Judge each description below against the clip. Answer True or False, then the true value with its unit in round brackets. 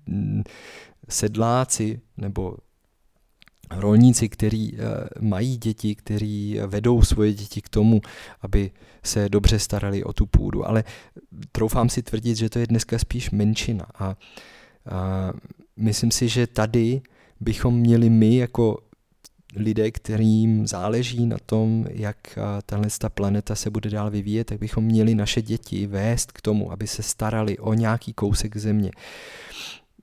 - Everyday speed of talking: True (130 wpm)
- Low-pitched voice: True (110 Hz)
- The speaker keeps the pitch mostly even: True (1.8 semitones)